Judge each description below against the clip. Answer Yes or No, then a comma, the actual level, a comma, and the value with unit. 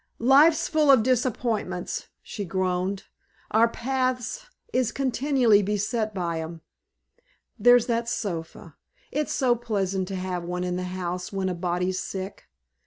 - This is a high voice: Yes, high, 205 Hz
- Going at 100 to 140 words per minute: Yes, slow, 135 wpm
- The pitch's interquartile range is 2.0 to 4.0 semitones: No, average, 5.2 semitones